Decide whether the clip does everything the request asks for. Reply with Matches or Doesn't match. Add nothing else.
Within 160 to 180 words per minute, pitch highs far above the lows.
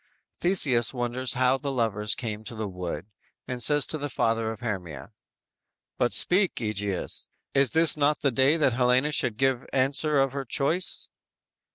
Doesn't match